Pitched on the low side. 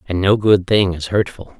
Yes: very low, 95 Hz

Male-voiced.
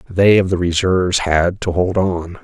Yes: male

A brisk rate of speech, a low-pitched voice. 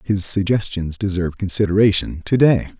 No: slow, 130 wpm; very low, 95 Hz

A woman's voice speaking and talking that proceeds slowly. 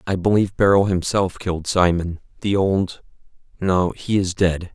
No: male; slow, 125 wpm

